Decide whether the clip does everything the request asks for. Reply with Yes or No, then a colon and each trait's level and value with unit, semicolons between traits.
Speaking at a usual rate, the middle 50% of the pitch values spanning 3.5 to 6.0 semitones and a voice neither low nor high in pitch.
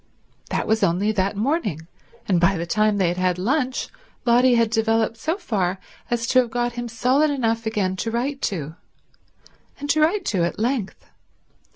No: average, 180 wpm; average, 4.8 semitones; high, 225 Hz